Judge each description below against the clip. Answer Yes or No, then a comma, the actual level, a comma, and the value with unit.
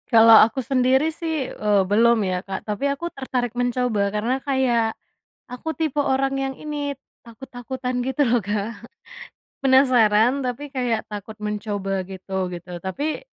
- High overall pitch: Yes, high, 245 Hz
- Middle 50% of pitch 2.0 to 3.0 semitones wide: No, average, 4.1 semitones